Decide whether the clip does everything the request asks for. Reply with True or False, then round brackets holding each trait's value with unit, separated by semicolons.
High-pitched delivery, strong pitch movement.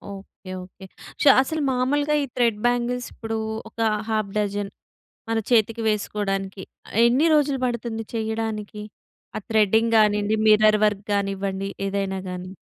False (215 Hz; 2.9 semitones)